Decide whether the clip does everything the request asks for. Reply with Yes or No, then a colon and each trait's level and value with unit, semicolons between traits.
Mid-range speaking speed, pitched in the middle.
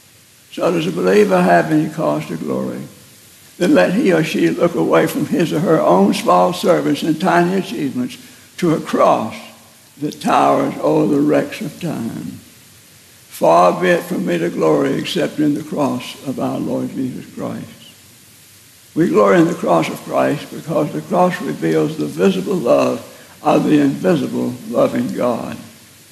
Yes: average, 165 wpm; medium, 150 Hz